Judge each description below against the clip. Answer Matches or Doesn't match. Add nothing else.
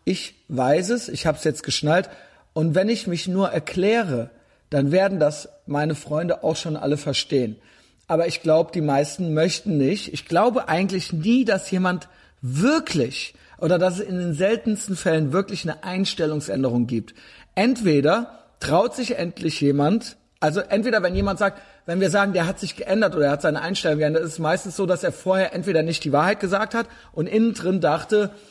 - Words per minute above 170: Matches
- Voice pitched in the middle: Matches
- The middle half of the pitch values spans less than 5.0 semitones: Matches